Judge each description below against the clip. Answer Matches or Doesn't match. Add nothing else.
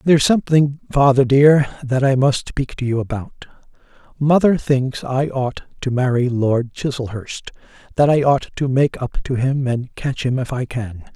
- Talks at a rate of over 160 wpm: Matches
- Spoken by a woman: Doesn't match